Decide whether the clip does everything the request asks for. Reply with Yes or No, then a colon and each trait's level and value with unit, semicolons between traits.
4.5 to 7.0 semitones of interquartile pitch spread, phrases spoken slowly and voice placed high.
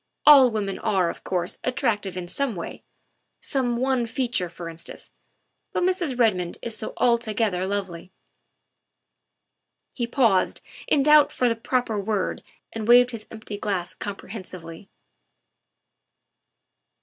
Yes: average, 4.8 semitones; slow, 125 wpm; high, 220 Hz